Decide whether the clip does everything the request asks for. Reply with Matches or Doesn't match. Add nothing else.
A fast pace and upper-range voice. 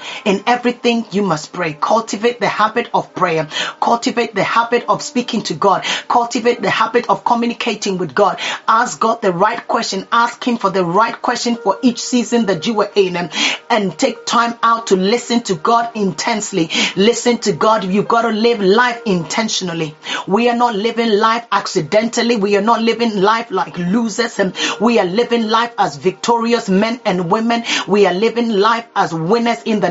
Doesn't match